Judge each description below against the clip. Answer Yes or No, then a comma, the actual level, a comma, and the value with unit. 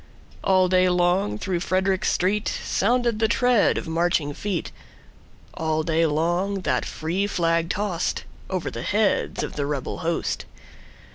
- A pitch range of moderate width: Yes, average, 3.3 semitones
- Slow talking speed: Yes, slow, 125 wpm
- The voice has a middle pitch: Yes, medium, 180 Hz